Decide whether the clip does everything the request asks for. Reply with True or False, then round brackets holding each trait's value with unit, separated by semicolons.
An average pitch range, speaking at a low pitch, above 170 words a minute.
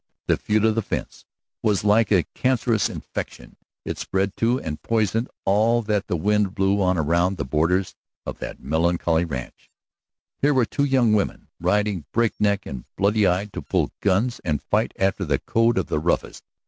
True (4.1 semitones; 100 Hz; 180 wpm)